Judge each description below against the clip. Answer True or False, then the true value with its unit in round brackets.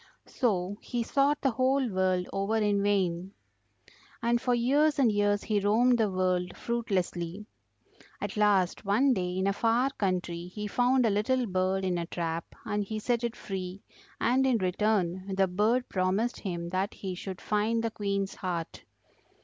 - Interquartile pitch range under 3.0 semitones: False (4.1 semitones)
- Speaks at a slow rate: False (165 wpm)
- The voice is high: True (205 Hz)